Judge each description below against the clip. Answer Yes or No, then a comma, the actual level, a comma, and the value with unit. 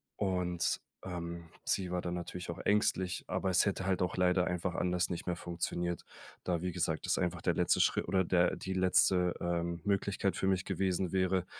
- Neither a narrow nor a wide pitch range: No, narrow, 1.2 semitones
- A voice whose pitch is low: Yes, very low, 90 Hz